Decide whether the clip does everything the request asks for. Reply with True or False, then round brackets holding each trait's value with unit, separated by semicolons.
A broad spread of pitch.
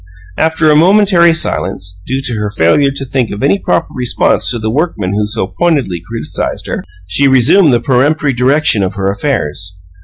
True (6.7 semitones)